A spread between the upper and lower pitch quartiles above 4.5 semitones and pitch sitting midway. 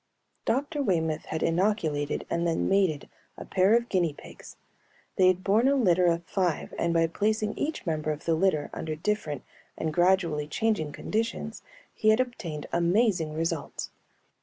Yes: average, 4.9 semitones; medium, 175 Hz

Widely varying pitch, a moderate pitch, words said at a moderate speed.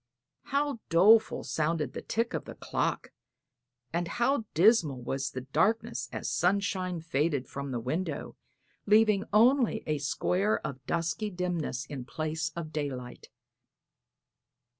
No: wide, 6.9 semitones; medium, 165 Hz; slow, 125 wpm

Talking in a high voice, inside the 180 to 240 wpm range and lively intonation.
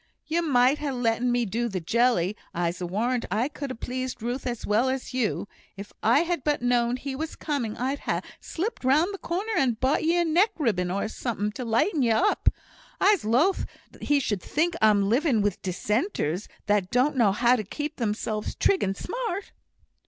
Yes: high, 245 Hz; average, 190 wpm; wide, 5.7 semitones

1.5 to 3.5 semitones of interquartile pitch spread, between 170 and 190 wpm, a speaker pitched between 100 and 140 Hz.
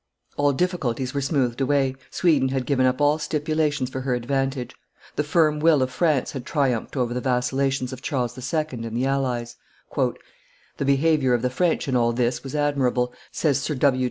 Yes: average, 2.7 semitones; average, 185 wpm; low, 135 Hz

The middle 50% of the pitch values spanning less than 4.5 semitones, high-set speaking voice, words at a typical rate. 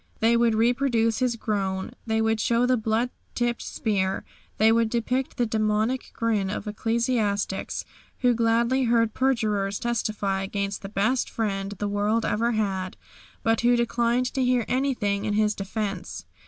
Yes: narrow, 2.5 semitones; high, 225 Hz; average, 155 wpm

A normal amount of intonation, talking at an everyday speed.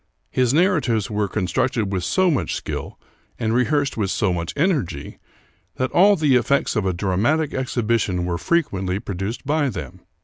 No: wide, 7.0 semitones; average, 170 wpm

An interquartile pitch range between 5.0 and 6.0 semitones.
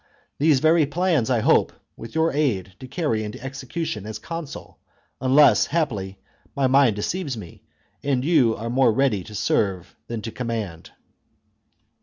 Yes: wide, 5.4 semitones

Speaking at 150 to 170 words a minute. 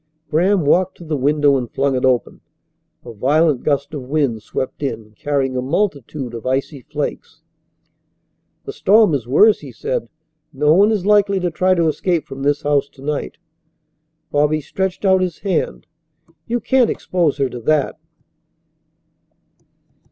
Yes: average, 155 wpm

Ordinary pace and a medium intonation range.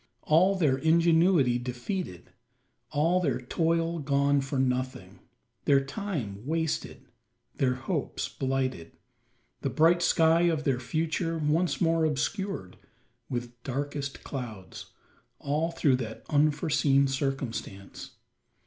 No: slow, 105 wpm; average, 4.3 semitones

